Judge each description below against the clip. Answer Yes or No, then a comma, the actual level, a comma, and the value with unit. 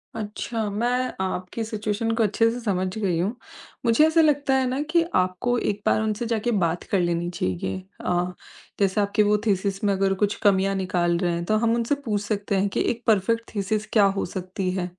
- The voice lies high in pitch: Yes, high, 205 Hz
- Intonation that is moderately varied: Yes, average, 3.5 semitones